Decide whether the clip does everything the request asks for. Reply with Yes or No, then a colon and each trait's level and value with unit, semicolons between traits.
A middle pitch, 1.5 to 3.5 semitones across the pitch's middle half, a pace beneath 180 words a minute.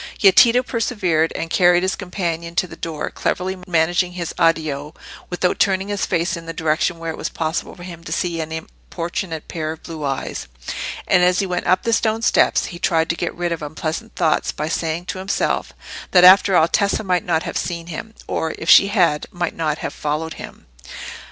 No: medium, 170 Hz; narrow, 2.5 semitones; fast, 205 wpm